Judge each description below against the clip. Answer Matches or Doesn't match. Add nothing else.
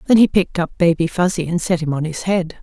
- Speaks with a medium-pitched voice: Matches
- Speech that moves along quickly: Matches